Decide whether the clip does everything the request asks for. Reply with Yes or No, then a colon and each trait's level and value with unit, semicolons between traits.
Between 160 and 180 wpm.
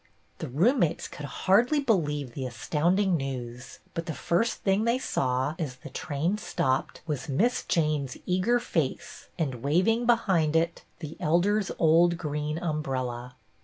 No: average, 145 wpm